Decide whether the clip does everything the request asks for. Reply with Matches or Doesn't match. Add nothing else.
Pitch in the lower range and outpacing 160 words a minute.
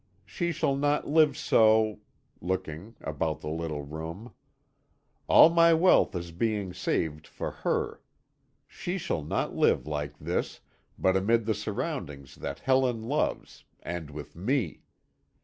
Doesn't match